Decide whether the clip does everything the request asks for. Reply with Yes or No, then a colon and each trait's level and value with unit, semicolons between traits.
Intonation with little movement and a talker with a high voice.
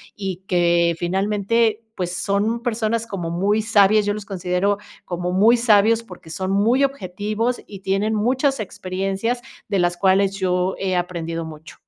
No: average, 3.3 semitones; high, 195 Hz